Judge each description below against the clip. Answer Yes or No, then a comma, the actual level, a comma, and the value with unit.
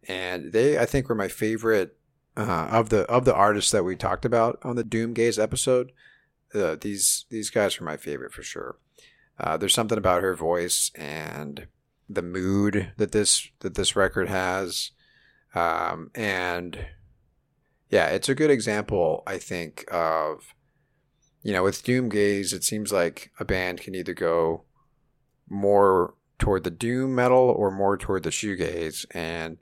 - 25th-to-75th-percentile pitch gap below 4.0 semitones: No, average, 4.3 semitones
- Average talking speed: Yes, average, 160 wpm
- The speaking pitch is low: Yes, low, 100 Hz